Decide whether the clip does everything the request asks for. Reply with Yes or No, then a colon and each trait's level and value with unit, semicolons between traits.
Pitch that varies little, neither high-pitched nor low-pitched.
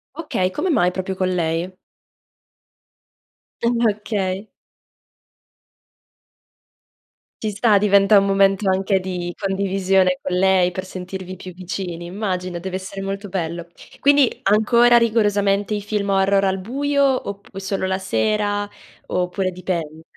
No: narrow, 1.9 semitones; high, 195 Hz